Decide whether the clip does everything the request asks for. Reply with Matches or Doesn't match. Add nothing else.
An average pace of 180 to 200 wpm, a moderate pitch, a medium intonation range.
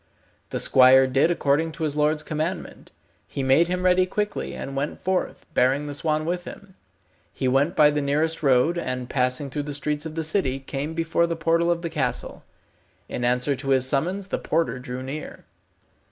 Matches